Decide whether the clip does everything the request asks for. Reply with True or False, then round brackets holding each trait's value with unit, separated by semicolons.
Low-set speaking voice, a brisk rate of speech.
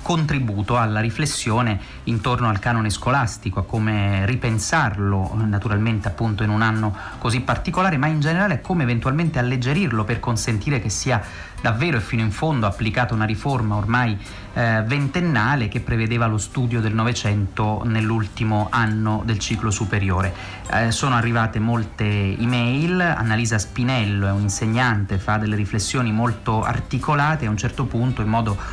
False (115 Hz; 150 wpm)